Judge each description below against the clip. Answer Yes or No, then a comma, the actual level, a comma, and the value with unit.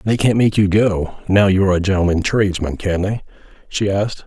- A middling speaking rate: No, fast, 210 wpm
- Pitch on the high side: No, very low, 95 Hz